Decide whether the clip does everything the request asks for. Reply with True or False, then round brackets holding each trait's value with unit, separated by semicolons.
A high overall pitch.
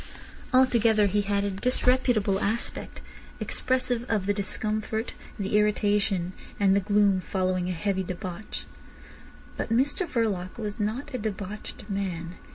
True (205 Hz)